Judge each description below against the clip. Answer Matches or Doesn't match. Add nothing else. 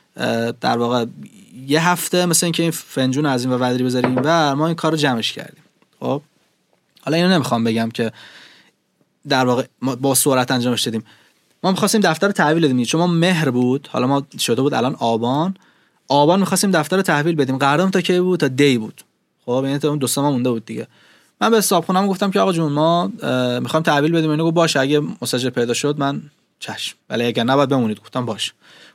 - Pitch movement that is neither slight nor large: Matches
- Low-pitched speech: Doesn't match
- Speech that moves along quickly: Matches